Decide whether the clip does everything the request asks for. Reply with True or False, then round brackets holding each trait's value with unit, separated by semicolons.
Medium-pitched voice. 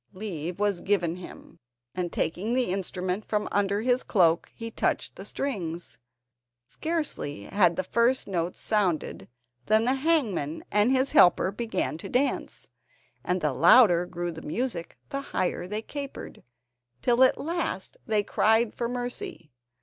False (205 Hz)